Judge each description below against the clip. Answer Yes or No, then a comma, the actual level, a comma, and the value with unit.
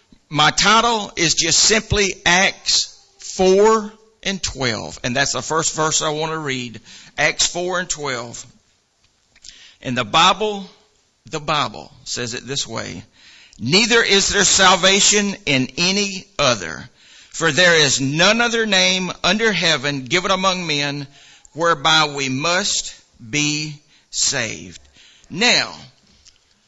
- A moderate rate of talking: No, slow, 125 wpm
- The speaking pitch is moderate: Yes, medium, 165 Hz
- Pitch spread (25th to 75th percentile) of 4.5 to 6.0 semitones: Yes, wide, 5.5 semitones